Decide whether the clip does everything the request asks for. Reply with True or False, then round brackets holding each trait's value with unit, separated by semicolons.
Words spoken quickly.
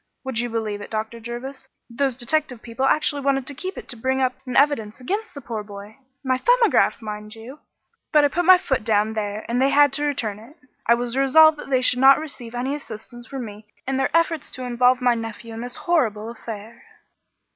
True (215 wpm)